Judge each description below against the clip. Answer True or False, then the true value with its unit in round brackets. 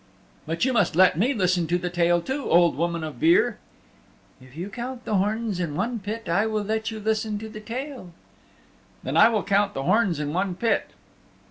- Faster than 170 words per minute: True (205 wpm)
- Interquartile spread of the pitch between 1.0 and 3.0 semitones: False (4.5 semitones)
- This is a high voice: True (205 Hz)